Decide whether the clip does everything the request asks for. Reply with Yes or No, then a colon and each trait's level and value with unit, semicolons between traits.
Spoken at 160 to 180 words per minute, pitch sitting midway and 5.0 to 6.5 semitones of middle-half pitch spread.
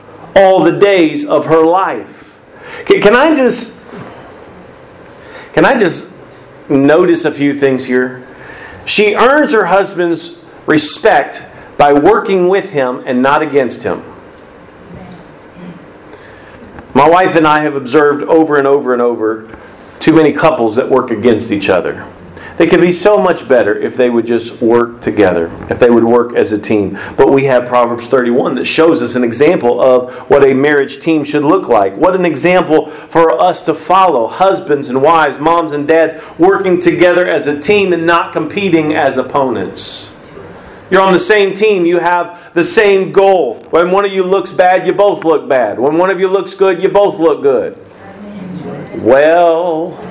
Yes: average, 170 wpm; medium, 165 Hz; wide, 5.6 semitones